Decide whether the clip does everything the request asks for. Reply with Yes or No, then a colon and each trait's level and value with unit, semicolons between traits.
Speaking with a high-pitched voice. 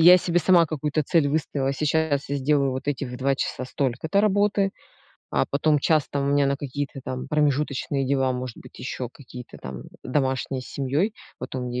No: medium, 140 Hz